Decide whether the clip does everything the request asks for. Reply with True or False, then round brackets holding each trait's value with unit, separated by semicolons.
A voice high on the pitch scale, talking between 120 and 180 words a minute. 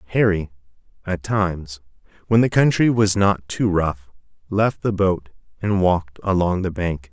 False (95 Hz; 150 wpm)